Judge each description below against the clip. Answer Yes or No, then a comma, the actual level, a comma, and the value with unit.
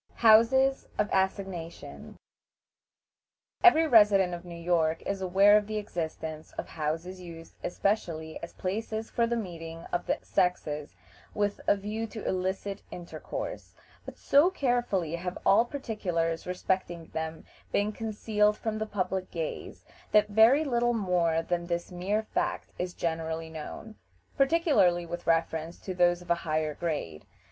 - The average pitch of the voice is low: No, medium, 185 Hz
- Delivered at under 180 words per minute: Yes, average, 140 wpm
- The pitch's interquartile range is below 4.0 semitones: No, average, 4.4 semitones